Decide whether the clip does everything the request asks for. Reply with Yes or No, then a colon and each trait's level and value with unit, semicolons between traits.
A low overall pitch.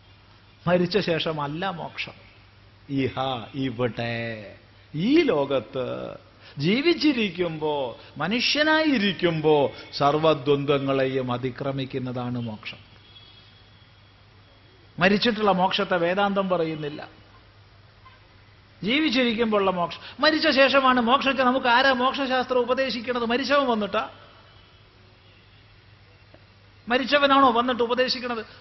No: medium, 145 Hz